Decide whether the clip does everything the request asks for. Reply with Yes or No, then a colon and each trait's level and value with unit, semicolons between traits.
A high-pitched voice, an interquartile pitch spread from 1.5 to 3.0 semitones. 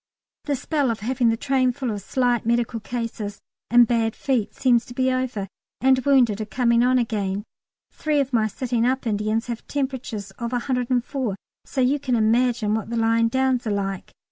Yes: high, 240 Hz; average, 2.7 semitones